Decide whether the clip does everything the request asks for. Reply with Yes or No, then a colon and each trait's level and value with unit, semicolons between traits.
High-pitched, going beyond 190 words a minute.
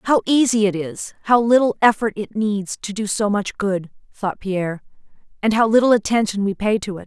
Yes: high, 210 Hz; fast, 205 wpm